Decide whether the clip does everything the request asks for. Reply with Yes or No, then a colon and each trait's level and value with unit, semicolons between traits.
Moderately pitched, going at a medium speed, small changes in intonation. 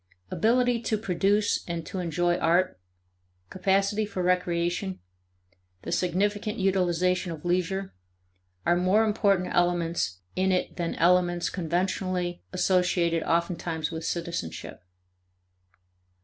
No: medium, 180 Hz; slow, 105 wpm; narrow, 2.1 semitones